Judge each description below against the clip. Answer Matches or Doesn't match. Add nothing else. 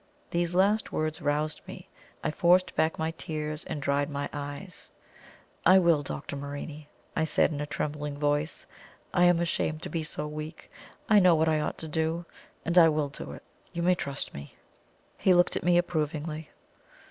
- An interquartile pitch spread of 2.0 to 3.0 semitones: Matches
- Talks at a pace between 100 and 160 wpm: Doesn't match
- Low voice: Doesn't match